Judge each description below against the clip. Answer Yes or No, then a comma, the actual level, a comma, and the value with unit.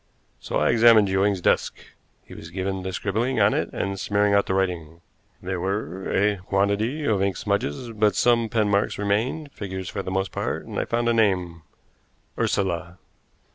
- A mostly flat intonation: Yes, narrow, 2.3 semitones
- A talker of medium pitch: No, low, 100 Hz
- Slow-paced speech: No, average, 175 wpm